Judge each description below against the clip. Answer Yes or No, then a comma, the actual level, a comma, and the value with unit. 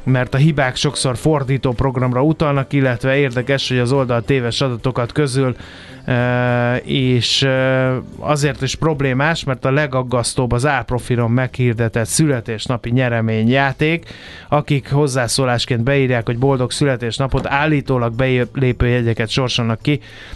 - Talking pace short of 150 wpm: Yes, average, 110 wpm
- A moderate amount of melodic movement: No, narrow, 2.1 semitones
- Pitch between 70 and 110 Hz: No, low, 130 Hz